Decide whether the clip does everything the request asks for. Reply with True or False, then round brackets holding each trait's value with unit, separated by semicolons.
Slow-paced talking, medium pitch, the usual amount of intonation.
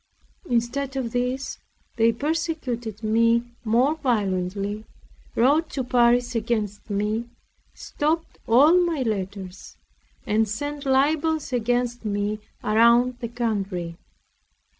False (100 wpm; 235 Hz; 3.9 semitones)